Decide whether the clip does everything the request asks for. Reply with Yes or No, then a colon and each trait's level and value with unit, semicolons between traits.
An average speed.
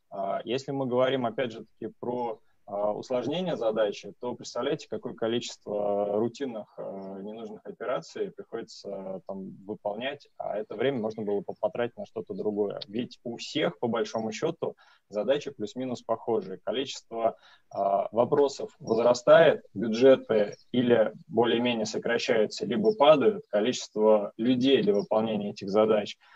Yes: average, 130 wpm